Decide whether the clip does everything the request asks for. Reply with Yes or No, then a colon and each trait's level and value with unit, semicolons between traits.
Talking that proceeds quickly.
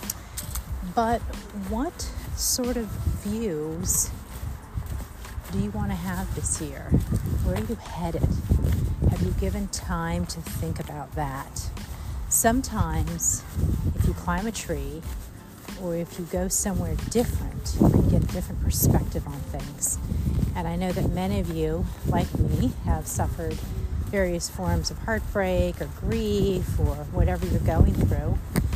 No: slow, 135 wpm